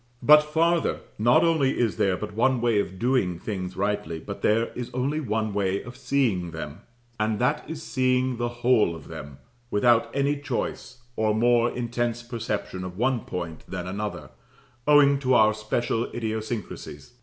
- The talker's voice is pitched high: No, low, 115 Hz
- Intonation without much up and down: No, average, 4.2 semitones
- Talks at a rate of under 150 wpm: No, average, 165 wpm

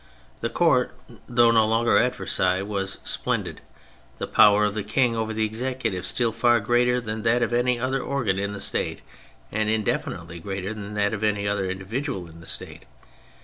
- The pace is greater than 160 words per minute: Yes, average, 185 wpm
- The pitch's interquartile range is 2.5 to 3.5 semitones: Yes, average, 3.0 semitones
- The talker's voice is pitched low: Yes, low, 110 Hz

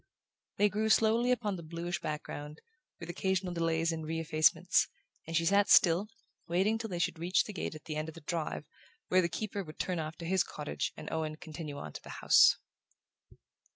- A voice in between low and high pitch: Yes, medium, 170 Hz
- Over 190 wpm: Yes, average, 200 wpm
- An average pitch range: Yes, average, 3.3 semitones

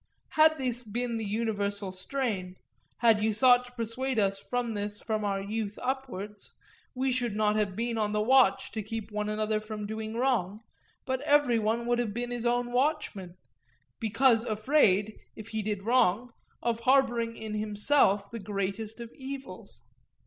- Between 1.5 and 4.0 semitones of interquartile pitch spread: Yes, average, 2.8 semitones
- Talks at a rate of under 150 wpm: No, average, 165 wpm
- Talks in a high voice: Yes, high, 225 Hz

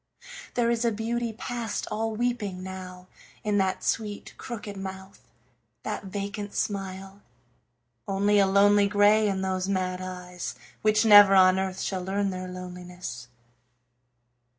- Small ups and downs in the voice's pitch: Yes, narrow, 2.0 semitones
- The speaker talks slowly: Yes, slow, 130 wpm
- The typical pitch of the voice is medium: No, high, 195 Hz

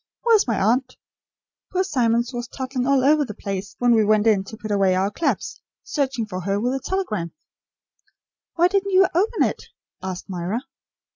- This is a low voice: No, high, 235 Hz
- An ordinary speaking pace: Yes, average, 185 wpm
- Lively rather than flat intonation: Yes, wide, 5.8 semitones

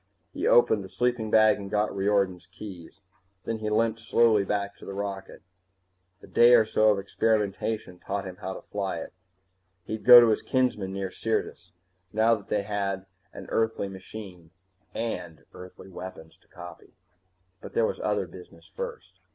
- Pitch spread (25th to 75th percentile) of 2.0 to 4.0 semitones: Yes, average, 2.7 semitones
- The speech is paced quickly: No, average, 165 wpm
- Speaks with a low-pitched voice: Yes, low, 105 Hz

